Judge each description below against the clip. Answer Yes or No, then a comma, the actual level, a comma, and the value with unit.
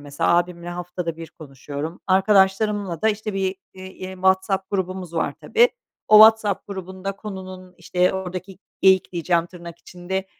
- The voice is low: No, medium, 185 Hz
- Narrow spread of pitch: Yes, narrow, 1.8 semitones